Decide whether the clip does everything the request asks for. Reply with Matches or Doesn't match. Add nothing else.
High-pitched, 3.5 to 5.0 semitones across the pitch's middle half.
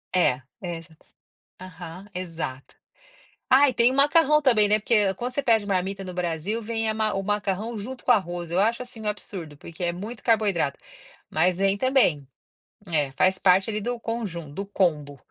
Matches